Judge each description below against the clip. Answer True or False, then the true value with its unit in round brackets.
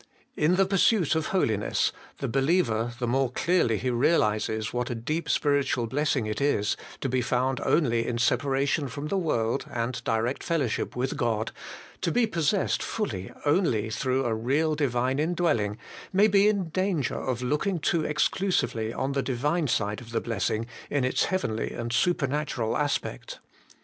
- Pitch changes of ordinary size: False (5.7 semitones)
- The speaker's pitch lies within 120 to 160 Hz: True (135 Hz)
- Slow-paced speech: False (165 wpm)